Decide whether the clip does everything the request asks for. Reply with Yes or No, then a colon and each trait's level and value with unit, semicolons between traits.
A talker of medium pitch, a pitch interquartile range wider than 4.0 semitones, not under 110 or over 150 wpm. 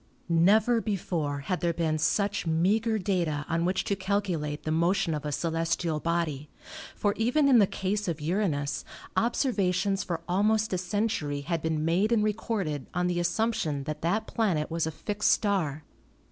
No: medium, 180 Hz; average, 4.6 semitones; average, 165 wpm